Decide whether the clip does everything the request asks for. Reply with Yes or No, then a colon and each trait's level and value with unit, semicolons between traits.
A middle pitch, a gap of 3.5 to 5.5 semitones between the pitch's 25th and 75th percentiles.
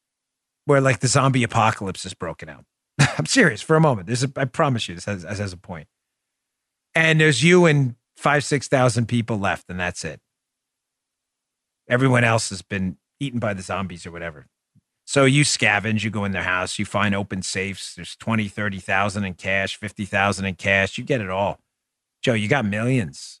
No: low, 105 Hz; average, 5.0 semitones